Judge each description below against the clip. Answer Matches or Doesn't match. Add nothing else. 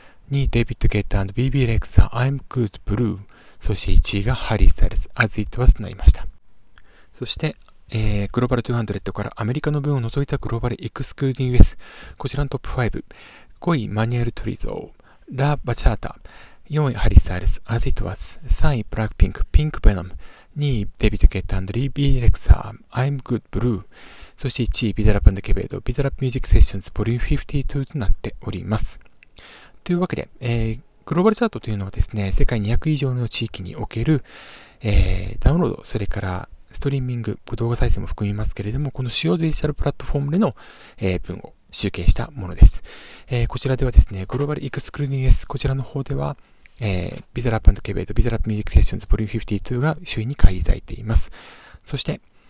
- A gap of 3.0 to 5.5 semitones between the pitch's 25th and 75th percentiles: Matches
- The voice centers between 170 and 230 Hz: Doesn't match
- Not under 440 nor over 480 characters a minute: Matches